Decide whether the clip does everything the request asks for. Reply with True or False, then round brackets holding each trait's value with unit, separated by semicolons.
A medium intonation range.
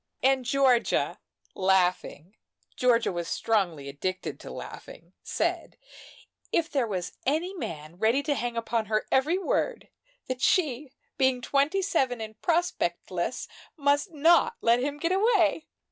False (6.3 semitones)